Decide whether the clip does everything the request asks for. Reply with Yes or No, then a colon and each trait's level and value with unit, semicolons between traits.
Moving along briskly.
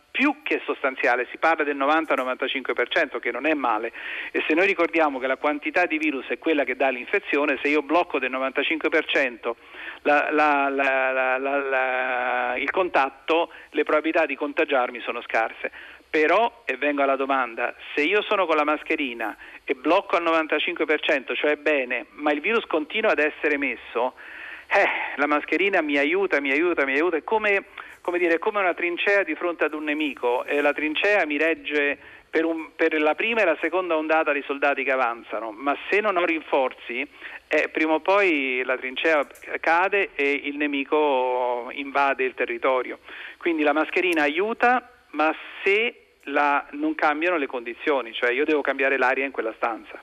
Yes: fast, 175 wpm